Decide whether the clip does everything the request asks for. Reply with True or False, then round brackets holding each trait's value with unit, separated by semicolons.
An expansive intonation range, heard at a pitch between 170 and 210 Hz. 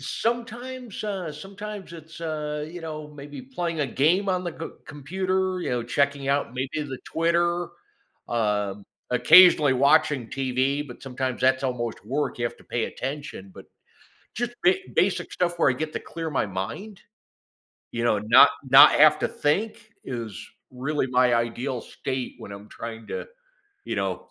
False (5.7 semitones; 145 Hz)